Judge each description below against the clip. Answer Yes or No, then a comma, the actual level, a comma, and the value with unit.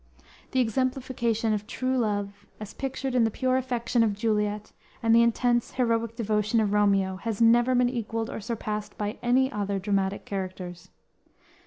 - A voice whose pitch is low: No, high, 225 Hz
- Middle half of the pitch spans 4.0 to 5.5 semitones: No, average, 2.8 semitones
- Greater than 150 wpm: Yes, average, 160 wpm